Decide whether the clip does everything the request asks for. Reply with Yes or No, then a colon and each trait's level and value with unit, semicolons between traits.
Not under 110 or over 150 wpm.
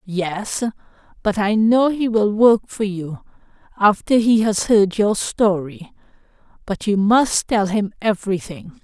Yes: slow, 135 wpm